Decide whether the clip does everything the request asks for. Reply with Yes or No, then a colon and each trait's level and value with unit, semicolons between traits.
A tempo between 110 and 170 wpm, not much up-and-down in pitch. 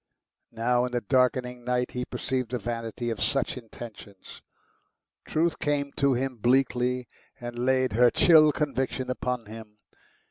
Yes: average, 140 wpm; narrow, 1.7 semitones